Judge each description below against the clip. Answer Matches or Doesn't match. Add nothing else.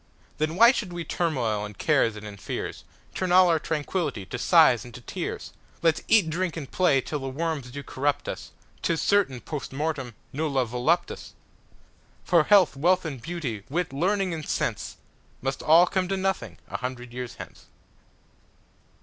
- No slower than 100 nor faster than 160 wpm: Matches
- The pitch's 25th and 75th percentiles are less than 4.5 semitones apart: Doesn't match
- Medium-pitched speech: Matches